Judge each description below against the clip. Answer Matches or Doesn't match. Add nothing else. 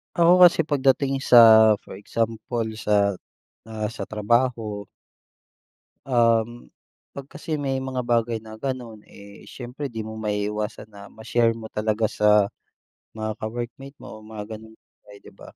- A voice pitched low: Matches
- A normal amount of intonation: Matches